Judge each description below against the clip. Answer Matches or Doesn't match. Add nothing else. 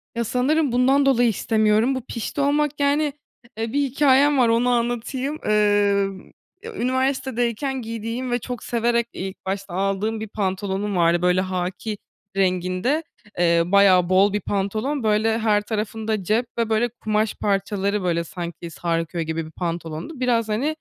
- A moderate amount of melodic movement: Matches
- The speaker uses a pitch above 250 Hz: Doesn't match